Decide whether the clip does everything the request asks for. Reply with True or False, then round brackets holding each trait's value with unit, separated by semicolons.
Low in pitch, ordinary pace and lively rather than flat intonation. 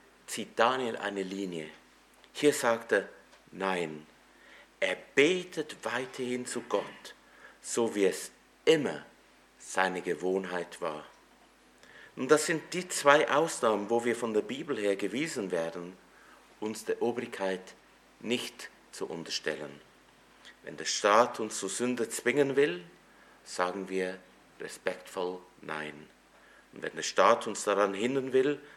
False (100 Hz; 125 wpm; 5.8 semitones)